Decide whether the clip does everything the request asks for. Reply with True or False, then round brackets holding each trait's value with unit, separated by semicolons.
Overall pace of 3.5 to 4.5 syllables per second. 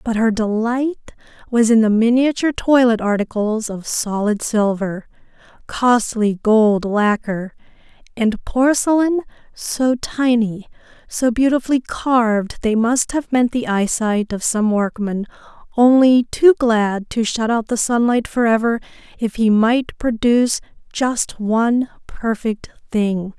True (4.0 syllables/s)